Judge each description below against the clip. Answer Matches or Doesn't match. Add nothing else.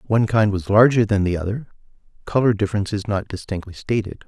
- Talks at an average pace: Matches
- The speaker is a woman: Doesn't match